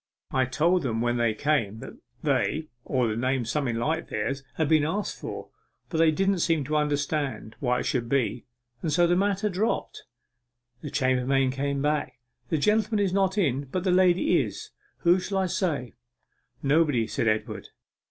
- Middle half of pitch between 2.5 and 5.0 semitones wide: No, wide, 5.5 semitones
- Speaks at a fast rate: No, average, 175 wpm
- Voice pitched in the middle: Yes, medium, 150 Hz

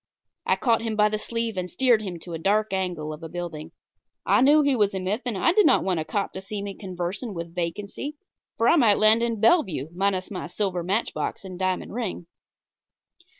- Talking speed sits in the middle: No, fast, 215 wpm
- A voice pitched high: Yes, high, 200 Hz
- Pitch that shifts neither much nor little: Yes, average, 4.1 semitones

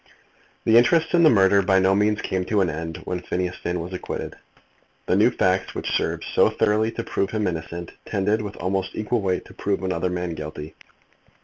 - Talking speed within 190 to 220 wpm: Yes, average, 200 wpm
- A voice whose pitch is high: No, very low, 95 Hz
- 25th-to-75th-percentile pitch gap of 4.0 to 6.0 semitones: No, average, 2.8 semitones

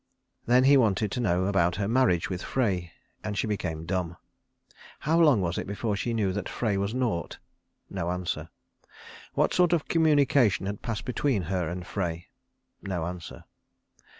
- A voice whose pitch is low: Yes, low, 100 Hz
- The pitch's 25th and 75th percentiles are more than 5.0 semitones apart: Yes, wide, 5.6 semitones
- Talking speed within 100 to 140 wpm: No, average, 165 wpm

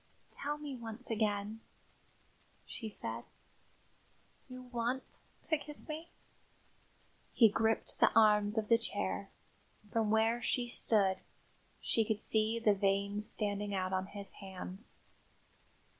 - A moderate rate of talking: No, slow, 120 wpm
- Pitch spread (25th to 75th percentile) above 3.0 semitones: No, narrow, 2.6 semitones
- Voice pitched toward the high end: Yes, high, 220 Hz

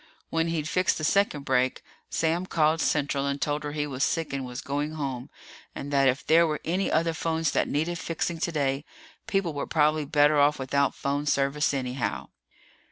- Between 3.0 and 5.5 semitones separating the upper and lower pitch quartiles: No, narrow, 2.6 semitones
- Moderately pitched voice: Yes, medium, 150 Hz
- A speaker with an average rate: Yes, average, 185 wpm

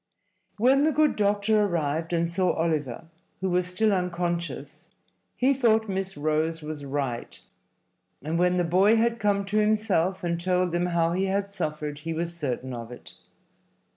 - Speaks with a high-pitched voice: No, medium, 175 Hz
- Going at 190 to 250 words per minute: No, average, 165 wpm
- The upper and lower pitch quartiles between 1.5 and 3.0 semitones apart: No, average, 4.0 semitones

